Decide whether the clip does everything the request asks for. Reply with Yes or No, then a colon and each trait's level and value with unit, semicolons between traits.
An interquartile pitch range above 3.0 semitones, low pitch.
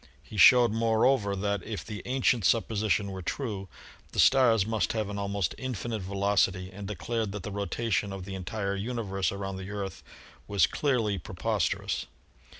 No: narrow, 2.6 semitones; low, 100 Hz